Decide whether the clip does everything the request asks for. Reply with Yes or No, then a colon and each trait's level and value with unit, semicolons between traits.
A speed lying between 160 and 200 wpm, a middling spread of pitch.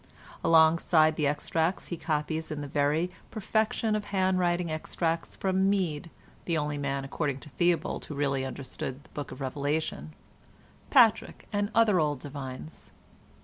No: average, 145 wpm; average, 3.9 semitones